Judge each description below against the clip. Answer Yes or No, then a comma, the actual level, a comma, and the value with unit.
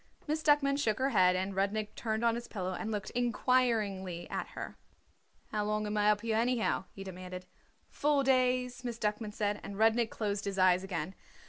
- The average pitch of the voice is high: Yes, high, 215 Hz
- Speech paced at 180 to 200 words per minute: Yes, average, 190 wpm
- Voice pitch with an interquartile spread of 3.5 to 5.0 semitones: Yes, average, 3.8 semitones